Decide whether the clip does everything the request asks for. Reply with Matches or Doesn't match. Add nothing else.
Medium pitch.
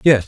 Doesn't match